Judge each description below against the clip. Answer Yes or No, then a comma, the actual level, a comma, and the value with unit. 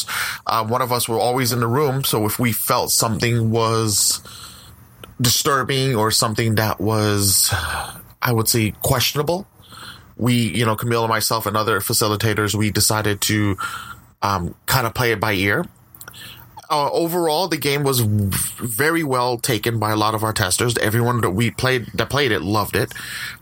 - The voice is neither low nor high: No, low, 115 Hz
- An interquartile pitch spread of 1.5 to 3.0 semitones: Yes, average, 2.7 semitones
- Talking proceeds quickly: No, average, 170 wpm